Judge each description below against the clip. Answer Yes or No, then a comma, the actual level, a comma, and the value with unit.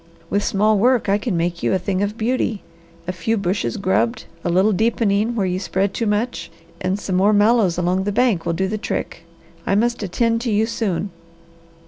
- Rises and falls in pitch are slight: No, average, 3.2 semitones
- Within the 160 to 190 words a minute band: No, average, 200 wpm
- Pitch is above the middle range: Yes, high, 205 Hz